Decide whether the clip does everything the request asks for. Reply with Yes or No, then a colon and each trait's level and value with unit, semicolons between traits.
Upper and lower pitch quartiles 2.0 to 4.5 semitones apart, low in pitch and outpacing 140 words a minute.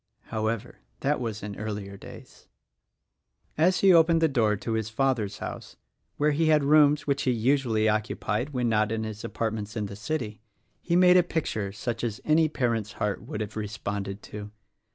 No: wide, 5.4 semitones; low, 115 Hz; average, 180 wpm